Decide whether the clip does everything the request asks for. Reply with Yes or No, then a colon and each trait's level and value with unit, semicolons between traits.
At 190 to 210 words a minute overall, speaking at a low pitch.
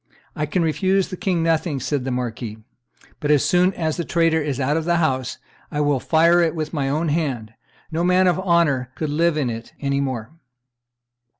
No: average, 200 wpm; medium, 155 Hz